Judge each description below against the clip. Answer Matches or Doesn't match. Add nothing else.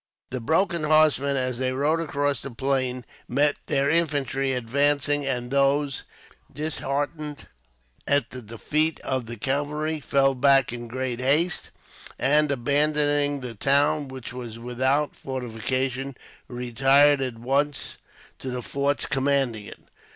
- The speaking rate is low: Matches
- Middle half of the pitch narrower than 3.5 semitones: Matches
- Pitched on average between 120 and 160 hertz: Matches